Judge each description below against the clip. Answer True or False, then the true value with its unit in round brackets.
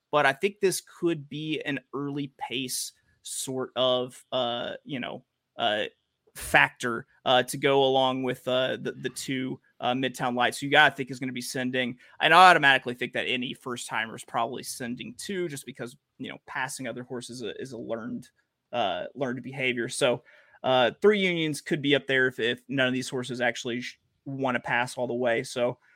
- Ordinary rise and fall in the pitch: False (2.3 semitones)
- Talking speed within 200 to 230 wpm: True (205 wpm)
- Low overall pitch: True (130 Hz)